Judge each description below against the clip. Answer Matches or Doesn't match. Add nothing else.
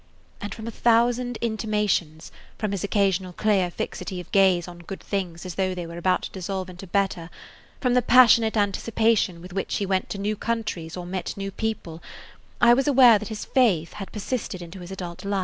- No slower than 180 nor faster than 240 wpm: Matches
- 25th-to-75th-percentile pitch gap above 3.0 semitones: Matches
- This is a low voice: Doesn't match